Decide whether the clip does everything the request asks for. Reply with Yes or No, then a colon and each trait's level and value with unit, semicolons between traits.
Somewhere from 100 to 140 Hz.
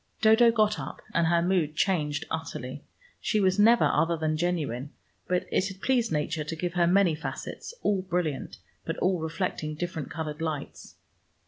No: medium, 170 Hz